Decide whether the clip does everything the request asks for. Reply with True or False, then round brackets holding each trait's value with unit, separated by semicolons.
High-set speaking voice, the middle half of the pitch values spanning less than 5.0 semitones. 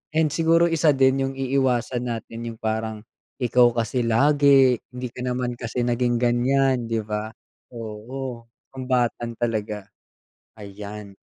False (120 Hz; 2.7 semitones)